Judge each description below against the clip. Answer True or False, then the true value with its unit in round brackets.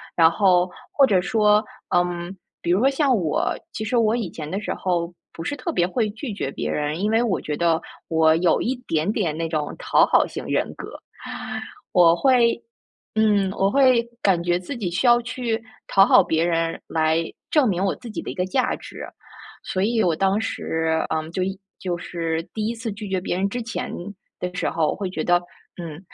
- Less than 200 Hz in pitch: True (185 Hz)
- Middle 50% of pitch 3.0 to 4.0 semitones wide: False (4.8 semitones)